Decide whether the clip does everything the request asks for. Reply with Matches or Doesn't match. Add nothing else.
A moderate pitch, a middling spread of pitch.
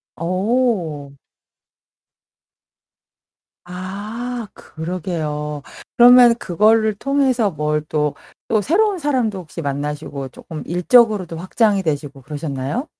Doesn't match